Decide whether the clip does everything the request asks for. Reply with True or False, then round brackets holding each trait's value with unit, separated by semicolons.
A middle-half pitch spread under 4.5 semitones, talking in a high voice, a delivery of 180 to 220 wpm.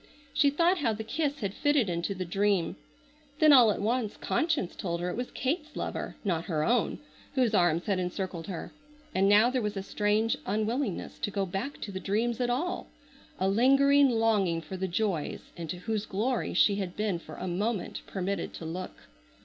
False (4.9 semitones; 205 Hz; 190 wpm)